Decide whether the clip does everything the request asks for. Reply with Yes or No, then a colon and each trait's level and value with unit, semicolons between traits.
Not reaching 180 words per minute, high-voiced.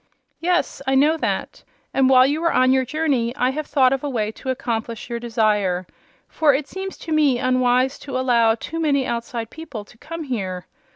No: average, 195 wpm; very high, 255 Hz